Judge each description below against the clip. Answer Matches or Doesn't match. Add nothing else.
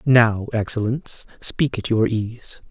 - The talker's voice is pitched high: Doesn't match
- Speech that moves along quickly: Doesn't match